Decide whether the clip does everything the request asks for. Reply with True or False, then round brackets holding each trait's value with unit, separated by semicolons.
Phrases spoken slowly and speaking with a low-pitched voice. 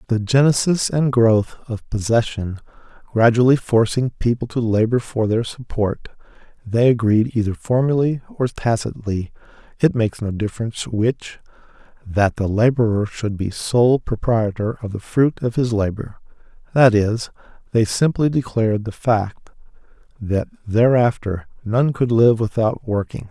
True (130 wpm; 115 Hz)